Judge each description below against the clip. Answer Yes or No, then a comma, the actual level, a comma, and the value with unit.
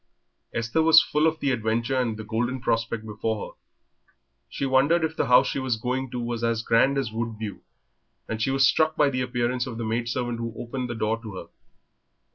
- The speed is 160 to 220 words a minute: Yes, fast, 205 wpm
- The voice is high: No, low, 120 Hz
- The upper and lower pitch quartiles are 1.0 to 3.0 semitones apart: Yes, average, 2.7 semitones